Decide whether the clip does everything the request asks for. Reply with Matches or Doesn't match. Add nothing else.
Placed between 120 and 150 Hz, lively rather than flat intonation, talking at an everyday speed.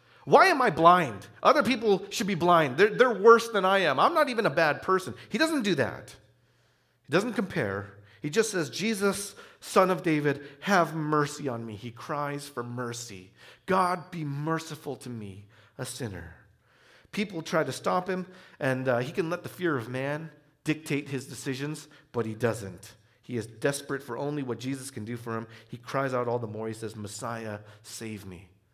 Matches